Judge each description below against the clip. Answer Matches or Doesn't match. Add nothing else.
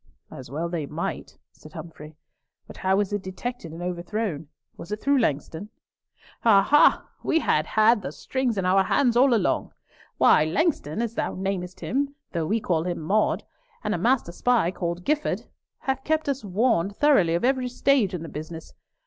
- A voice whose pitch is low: Doesn't match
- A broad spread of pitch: Matches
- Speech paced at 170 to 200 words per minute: Matches